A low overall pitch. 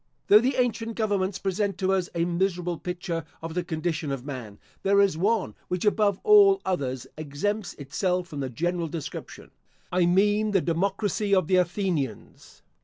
No: medium, 180 Hz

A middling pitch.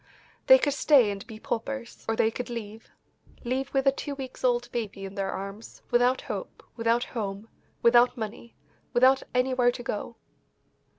No: high, 240 Hz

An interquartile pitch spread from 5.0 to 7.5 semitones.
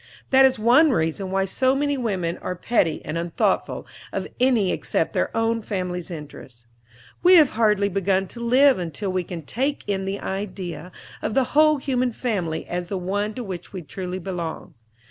Yes: wide, 5.6 semitones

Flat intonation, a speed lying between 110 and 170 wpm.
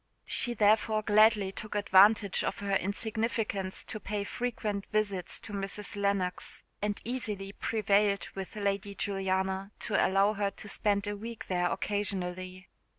Yes: narrow, 1.6 semitones; average, 140 wpm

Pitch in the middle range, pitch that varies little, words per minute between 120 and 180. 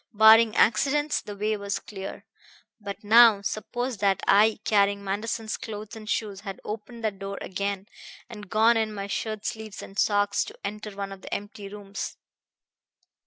No: high, 210 Hz; narrow, 1.7 semitones; average, 165 wpm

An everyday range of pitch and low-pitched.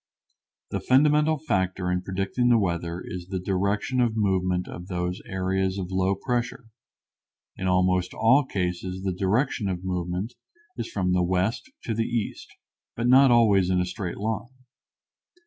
Yes: average, 4.0 semitones; very low, 95 Hz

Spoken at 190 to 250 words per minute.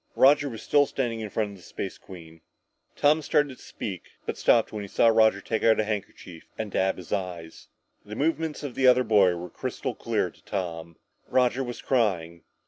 Yes: fast, 205 wpm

